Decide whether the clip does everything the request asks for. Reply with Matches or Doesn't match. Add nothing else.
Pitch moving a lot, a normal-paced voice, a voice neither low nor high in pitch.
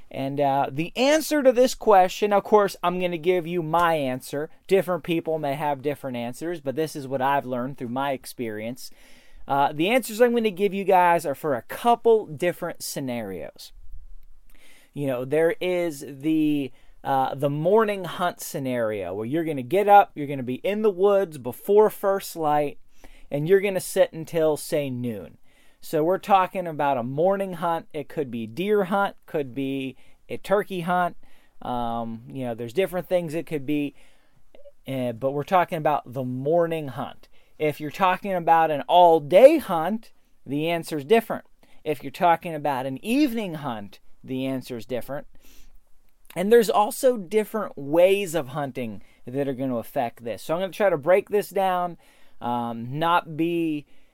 Matches